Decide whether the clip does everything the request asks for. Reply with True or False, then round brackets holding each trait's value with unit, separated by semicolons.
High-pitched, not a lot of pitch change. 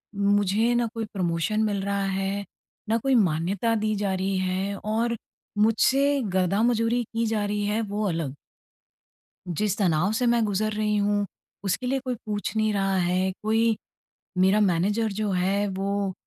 True (205 Hz; 2.3 semitones)